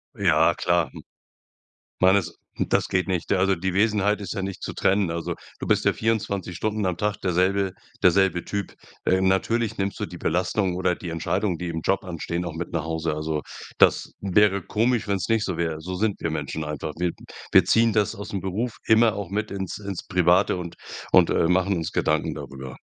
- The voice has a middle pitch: No, very low, 95 Hz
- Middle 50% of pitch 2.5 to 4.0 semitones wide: Yes, average, 2.9 semitones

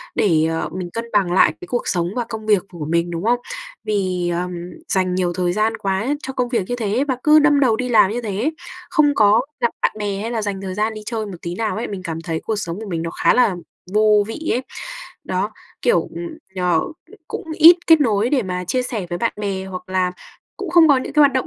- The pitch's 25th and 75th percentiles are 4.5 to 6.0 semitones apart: Yes, average, 5.0 semitones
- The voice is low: No, high, 210 Hz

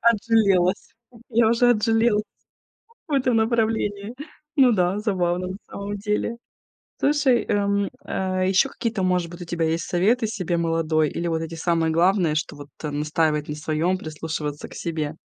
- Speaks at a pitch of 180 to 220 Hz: Yes, medium, 185 Hz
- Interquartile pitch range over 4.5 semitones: Yes, average, 5.2 semitones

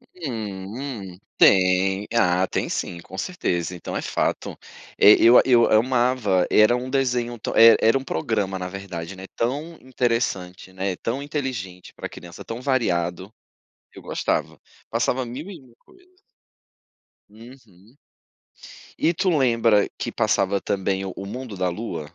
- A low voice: Yes, low, 110 Hz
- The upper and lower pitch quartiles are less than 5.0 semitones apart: No, average, 5.3 semitones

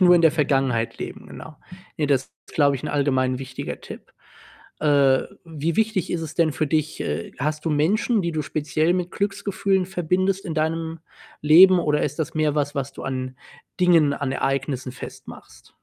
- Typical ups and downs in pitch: Yes, average, 3.8 semitones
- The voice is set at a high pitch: No, medium, 155 Hz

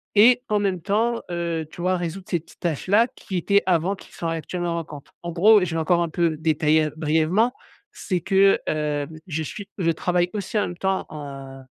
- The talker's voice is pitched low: No, medium, 175 Hz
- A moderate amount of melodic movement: Yes, average, 3.5 semitones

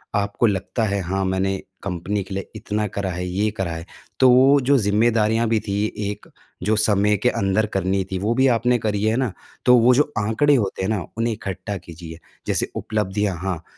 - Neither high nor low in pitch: No, low, 105 Hz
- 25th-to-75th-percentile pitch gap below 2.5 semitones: No, average, 2.8 semitones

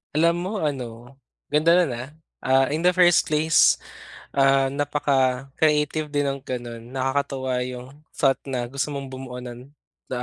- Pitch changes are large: No, average, 2.7 semitones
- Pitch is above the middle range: No, low, 135 Hz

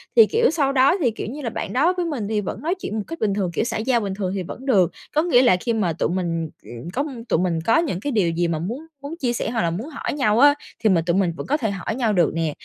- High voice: Yes, high, 220 Hz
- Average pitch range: No, wide, 7.4 semitones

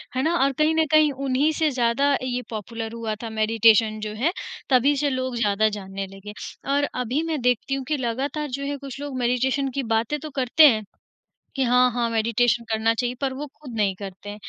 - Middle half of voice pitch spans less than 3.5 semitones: No, average, 3.9 semitones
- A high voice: Yes, very high, 250 Hz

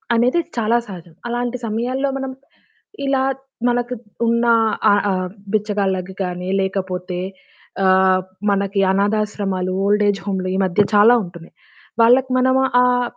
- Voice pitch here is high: Yes, high, 205 Hz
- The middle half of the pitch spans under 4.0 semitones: No, average, 4.4 semitones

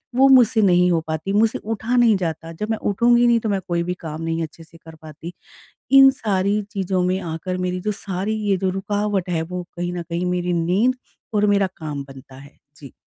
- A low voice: No, medium, 180 Hz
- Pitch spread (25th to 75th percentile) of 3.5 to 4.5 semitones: Yes, average, 4.2 semitones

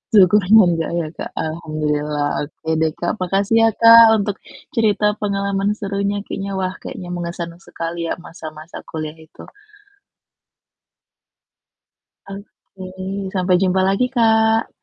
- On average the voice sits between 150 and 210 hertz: Yes, medium, 185 Hz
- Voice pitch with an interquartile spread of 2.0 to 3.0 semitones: No, average, 3.5 semitones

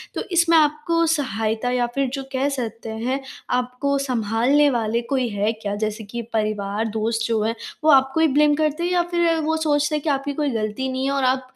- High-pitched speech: Yes, very high, 260 Hz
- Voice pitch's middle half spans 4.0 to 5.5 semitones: Yes, average, 4.7 semitones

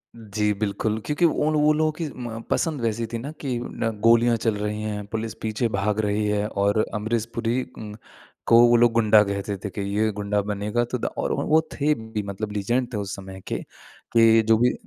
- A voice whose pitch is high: No, low, 110 Hz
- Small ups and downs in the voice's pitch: Yes, narrow, 2.3 semitones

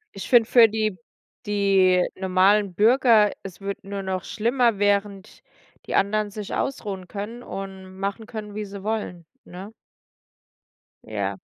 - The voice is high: Yes, high, 200 Hz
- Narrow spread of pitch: Yes, narrow, 2.1 semitones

